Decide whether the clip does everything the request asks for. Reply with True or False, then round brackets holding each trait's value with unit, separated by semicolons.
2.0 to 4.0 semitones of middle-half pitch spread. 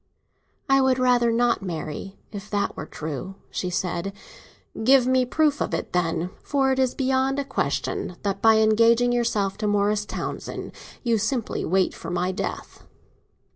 False (4.9 semitones)